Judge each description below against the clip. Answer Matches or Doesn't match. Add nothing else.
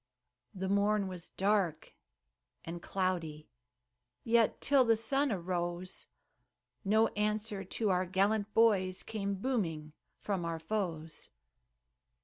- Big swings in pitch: Doesn't match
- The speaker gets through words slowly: Matches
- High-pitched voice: Matches